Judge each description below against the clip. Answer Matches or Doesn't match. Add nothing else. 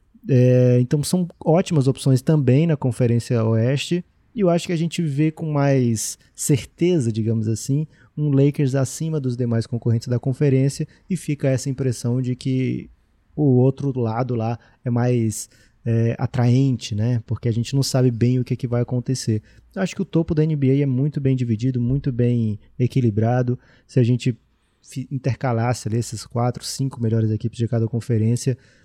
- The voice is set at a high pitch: Doesn't match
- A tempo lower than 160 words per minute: Doesn't match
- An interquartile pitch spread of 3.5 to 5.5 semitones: Doesn't match